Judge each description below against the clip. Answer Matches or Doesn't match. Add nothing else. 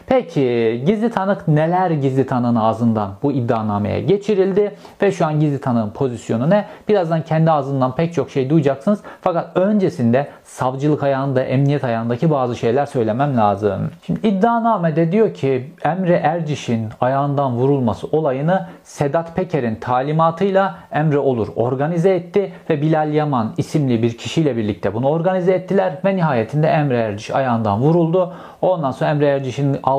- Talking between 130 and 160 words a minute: Matches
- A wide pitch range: Matches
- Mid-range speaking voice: Matches